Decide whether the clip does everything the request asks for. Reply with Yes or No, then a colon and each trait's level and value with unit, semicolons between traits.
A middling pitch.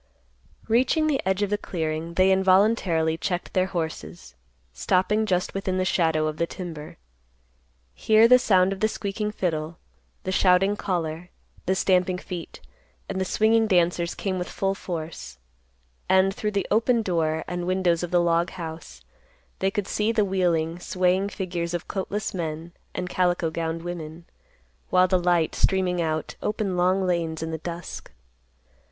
Yes: medium, 180 Hz